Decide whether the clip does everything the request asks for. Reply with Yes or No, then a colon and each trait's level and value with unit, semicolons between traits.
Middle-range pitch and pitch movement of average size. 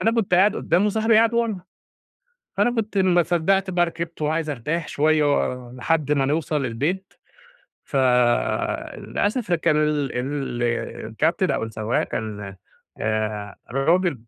No: medium, 155 Hz; wide, 6.5 semitones